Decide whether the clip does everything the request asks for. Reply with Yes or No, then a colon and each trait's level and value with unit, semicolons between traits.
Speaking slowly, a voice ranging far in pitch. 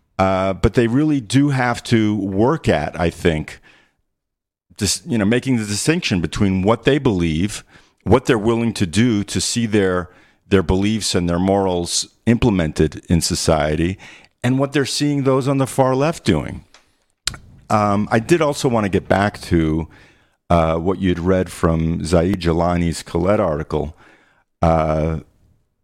No: average, 155 wpm; wide, 5.7 semitones